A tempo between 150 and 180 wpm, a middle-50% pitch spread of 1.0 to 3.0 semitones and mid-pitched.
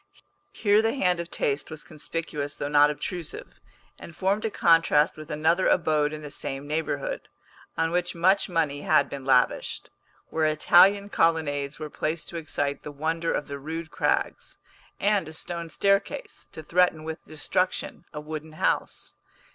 Yes: average, 160 wpm; average, 2.7 semitones; medium, 160 Hz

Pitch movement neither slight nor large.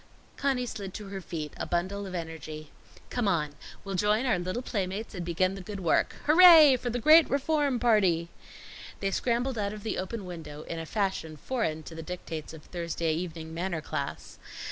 No: wide, 5.9 semitones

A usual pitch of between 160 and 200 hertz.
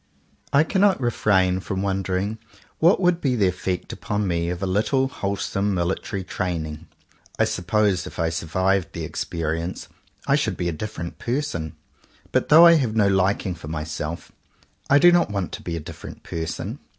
No: very low, 95 Hz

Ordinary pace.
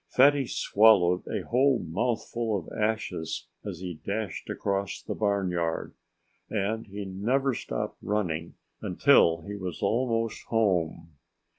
No: slow, 120 wpm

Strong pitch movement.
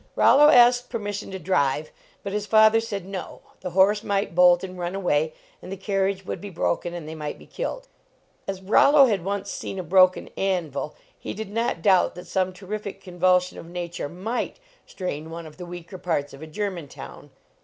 No: average, 2.8 semitones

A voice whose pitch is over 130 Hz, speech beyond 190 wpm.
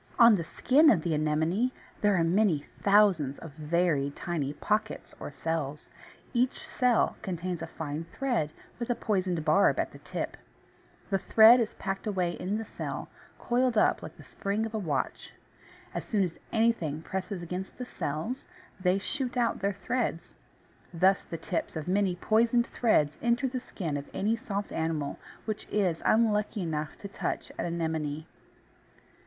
No: high, 190 Hz; average, 165 wpm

